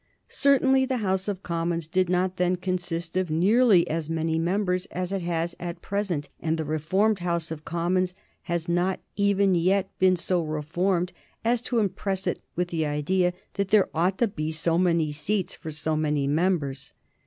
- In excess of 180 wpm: No, average, 175 wpm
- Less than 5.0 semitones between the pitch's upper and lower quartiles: Yes, average, 2.7 semitones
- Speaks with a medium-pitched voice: Yes, medium, 180 Hz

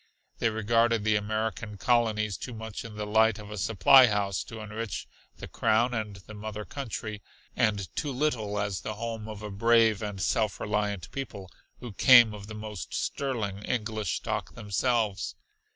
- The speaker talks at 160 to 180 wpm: Yes, average, 170 wpm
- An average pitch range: No, narrow, 1.8 semitones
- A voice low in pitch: Yes, low, 110 Hz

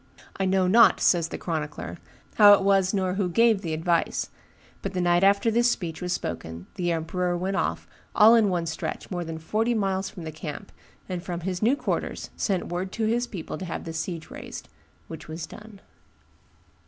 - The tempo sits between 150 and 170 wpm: No, average, 195 wpm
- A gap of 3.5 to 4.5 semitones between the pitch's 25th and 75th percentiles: No, average, 3.1 semitones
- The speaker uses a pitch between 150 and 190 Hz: Yes, medium, 185 Hz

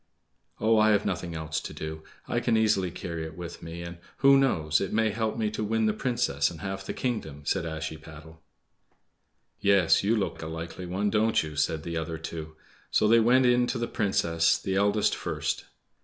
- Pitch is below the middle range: Yes, very low, 95 Hz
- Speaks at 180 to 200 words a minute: Yes, average, 190 wpm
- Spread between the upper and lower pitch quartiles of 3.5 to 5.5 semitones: Yes, average, 5.2 semitones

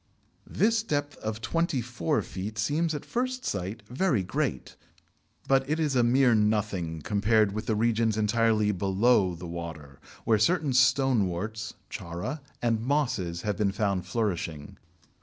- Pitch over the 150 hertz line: No, low, 110 Hz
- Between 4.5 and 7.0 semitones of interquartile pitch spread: Yes, average, 5.2 semitones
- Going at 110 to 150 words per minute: Yes, average, 140 wpm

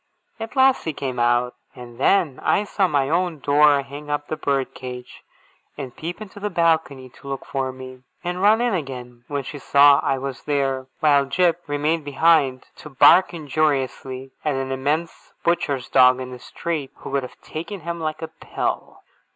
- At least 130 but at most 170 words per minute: No, average, 185 wpm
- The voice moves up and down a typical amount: Yes, average, 3.9 semitones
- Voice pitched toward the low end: No, medium, 145 Hz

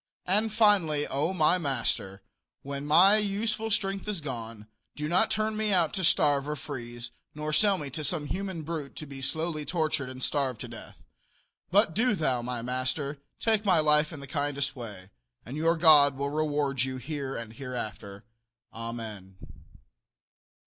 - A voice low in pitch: No, medium, 150 Hz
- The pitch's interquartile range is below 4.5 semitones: No, average, 5.3 semitones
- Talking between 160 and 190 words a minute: Yes, average, 165 wpm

